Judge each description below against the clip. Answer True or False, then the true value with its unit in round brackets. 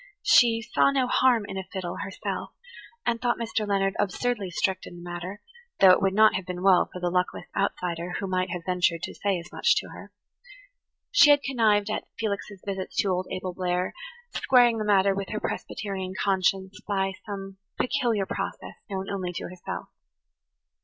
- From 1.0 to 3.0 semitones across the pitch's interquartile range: True (2.6 semitones)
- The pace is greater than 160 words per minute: True (180 wpm)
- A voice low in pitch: False (195 Hz)